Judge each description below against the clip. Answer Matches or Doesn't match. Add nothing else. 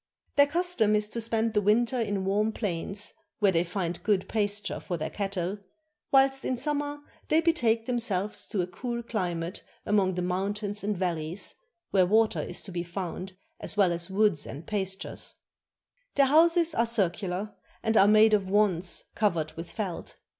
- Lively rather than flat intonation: Doesn't match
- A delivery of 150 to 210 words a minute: Matches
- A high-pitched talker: Matches